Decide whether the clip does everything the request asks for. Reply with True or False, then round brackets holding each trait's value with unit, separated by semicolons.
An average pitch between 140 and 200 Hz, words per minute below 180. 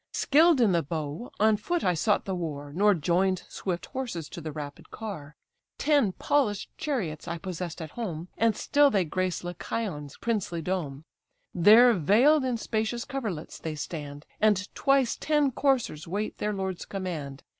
True (190 Hz; 160 wpm)